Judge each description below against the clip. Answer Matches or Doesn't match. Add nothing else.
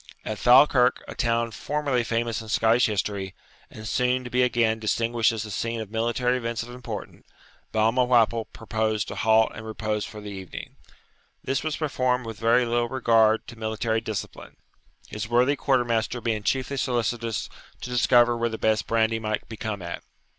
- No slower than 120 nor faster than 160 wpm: Doesn't match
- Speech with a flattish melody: Matches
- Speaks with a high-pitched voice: Doesn't match